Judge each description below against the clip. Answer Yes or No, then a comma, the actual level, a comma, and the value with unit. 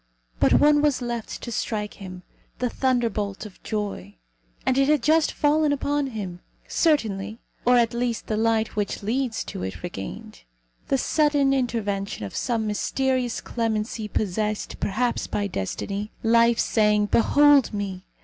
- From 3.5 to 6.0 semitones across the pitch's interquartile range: Yes, average, 4.1 semitones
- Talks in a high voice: Yes, high, 225 Hz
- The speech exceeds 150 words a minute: No, average, 145 wpm